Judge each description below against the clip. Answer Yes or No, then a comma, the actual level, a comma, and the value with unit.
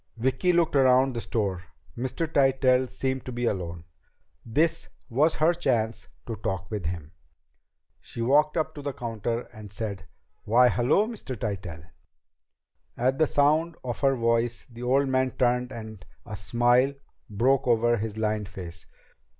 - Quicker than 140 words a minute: Yes, average, 150 wpm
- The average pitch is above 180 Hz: No, low, 120 Hz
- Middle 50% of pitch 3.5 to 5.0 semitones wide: Yes, average, 3.8 semitones